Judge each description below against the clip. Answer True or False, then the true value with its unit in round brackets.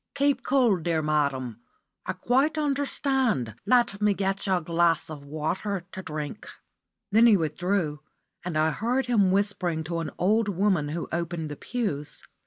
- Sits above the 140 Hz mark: True (185 Hz)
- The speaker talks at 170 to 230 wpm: False (160 wpm)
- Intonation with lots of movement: True (6.3 semitones)